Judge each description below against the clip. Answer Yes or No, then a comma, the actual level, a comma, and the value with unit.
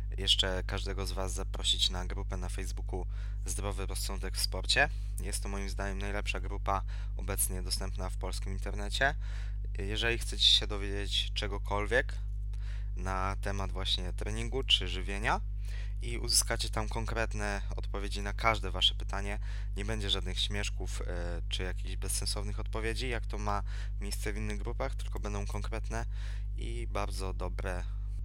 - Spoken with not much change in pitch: Yes, narrow, 1.0 semitones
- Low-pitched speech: Yes, low, 100 Hz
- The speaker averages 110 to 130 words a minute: No, average, 140 wpm